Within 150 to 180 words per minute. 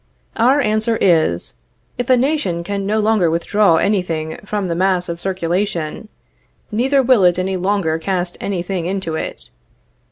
Yes: average, 160 wpm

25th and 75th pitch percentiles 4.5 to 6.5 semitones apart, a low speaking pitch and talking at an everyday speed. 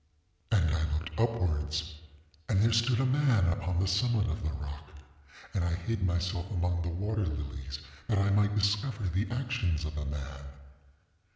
Yes: wide, 5.5 semitones; very low, 90 Hz; average, 170 wpm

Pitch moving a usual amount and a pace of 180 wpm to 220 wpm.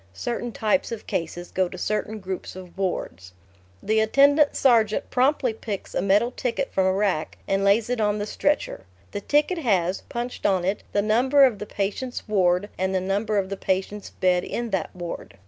Yes: average, 4.0 semitones; average, 190 wpm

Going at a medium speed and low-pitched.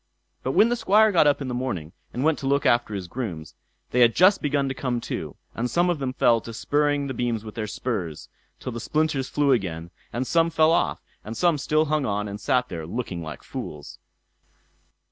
No: fast, 220 wpm; low, 125 Hz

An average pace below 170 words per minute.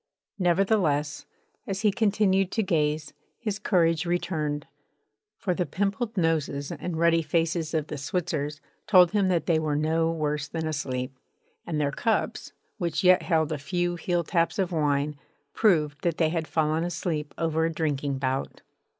Yes: average, 155 wpm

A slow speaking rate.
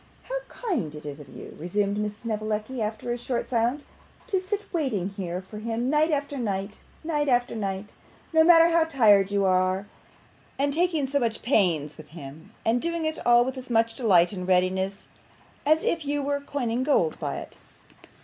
No: average, 185 wpm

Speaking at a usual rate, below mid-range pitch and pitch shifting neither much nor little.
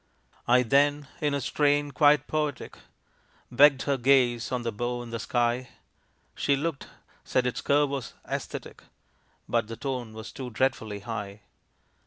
Yes: average, 150 wpm; low, 130 Hz; average, 3.2 semitones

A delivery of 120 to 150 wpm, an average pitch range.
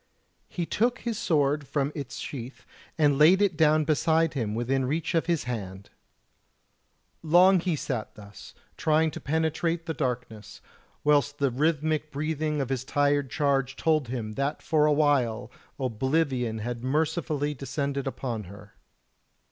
Yes: average, 145 wpm; average, 3.7 semitones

